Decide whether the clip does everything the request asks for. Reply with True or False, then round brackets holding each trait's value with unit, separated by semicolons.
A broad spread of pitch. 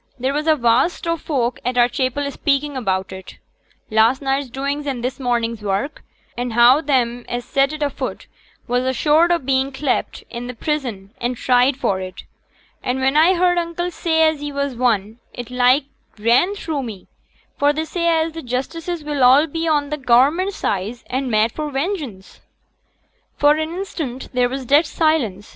False (4.0 semitones)